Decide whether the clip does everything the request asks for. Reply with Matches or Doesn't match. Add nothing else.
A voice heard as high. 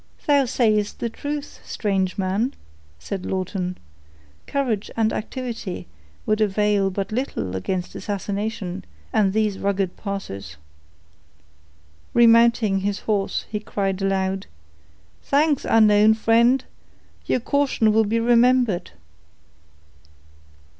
Matches